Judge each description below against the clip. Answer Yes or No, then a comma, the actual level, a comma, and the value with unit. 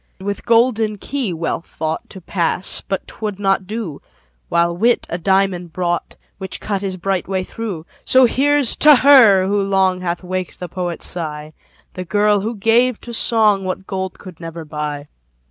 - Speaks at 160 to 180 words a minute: Yes, average, 170 wpm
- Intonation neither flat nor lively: Yes, average, 3.7 semitones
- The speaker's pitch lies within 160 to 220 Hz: Yes, high, 190 Hz